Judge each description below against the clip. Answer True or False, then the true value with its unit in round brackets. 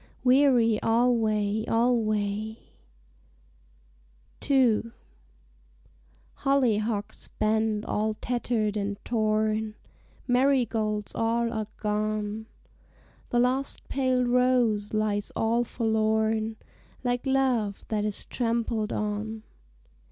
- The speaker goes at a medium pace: False (80 wpm)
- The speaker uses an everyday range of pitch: False (2.3 semitones)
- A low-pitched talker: False (220 Hz)